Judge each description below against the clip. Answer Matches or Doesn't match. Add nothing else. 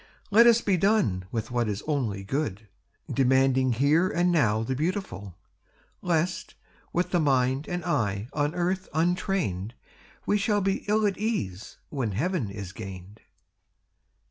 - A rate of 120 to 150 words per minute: Matches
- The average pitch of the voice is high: Doesn't match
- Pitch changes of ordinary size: Doesn't match